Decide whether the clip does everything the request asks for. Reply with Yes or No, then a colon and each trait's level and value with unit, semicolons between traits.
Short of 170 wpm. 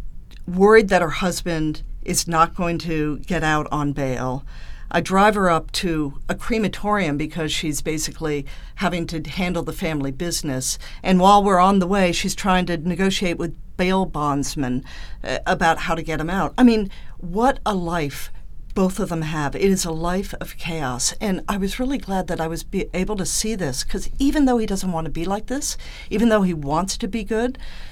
No: average, 200 wpm